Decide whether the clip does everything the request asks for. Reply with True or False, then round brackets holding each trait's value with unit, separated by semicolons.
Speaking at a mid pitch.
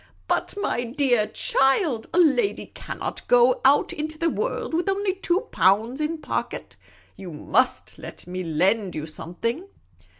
False (265 Hz)